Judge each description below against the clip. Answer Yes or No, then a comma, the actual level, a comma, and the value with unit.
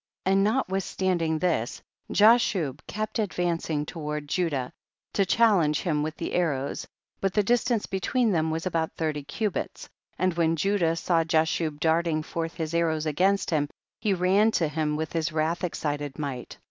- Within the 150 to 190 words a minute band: Yes, average, 160 wpm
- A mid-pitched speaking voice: Yes, medium, 165 Hz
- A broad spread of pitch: No, average, 3.6 semitones